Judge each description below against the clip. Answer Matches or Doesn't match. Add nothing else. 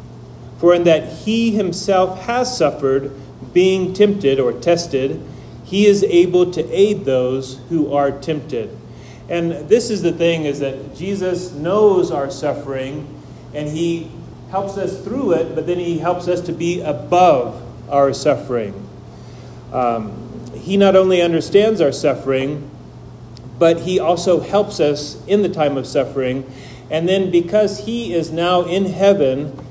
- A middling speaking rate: Matches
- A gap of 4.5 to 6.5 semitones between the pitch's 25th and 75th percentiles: Matches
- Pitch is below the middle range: Doesn't match